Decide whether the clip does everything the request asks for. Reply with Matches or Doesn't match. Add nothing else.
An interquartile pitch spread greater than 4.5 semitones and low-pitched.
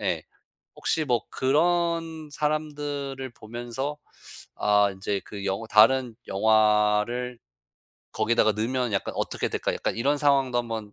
Matches